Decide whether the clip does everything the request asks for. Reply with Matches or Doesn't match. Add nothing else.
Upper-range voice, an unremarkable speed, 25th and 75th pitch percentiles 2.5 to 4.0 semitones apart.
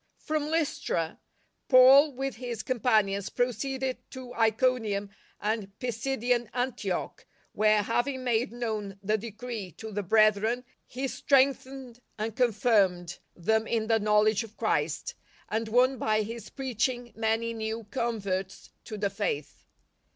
Doesn't match